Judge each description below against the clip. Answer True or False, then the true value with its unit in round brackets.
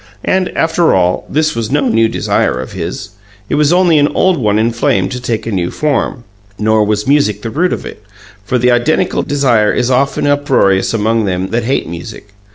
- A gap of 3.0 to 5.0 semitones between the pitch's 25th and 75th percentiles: False (5.4 semitones)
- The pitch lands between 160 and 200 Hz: False (120 Hz)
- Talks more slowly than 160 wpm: False (195 wpm)